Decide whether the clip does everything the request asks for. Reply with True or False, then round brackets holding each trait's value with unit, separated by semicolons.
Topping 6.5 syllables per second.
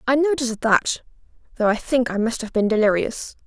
False (5.5 syllables/s)